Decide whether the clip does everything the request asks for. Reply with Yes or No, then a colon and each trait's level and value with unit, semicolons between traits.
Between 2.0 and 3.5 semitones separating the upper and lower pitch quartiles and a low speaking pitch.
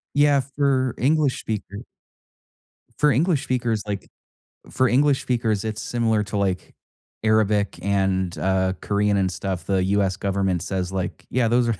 No: average, 4.7 semitones; low, 105 Hz